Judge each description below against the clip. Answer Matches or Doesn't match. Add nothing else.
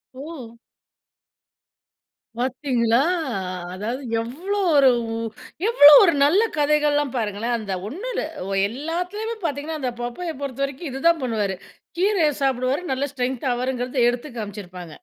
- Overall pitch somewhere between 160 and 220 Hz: Doesn't match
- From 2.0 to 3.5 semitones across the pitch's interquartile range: Doesn't match